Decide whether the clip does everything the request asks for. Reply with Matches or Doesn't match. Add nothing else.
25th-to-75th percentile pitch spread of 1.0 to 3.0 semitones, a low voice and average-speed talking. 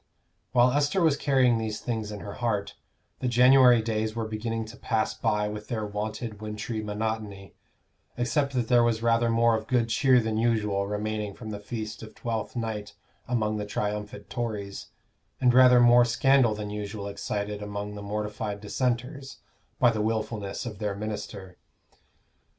Matches